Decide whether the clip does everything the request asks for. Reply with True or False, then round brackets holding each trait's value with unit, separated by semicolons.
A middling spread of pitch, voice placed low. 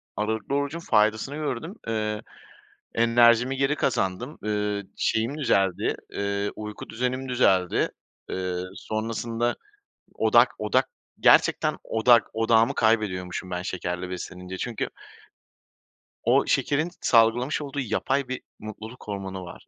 True (4.0 semitones; 110 Hz)